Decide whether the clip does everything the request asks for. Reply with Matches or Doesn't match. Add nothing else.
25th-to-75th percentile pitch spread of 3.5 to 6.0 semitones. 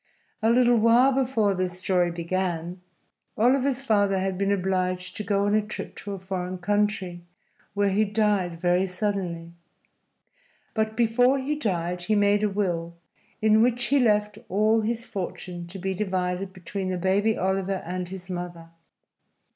Doesn't match